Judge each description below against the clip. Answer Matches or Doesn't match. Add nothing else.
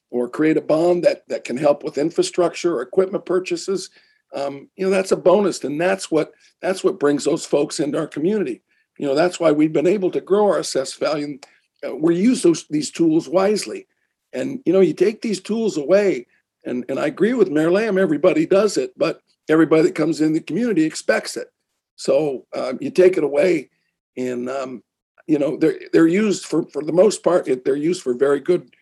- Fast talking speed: Matches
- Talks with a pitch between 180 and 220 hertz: Matches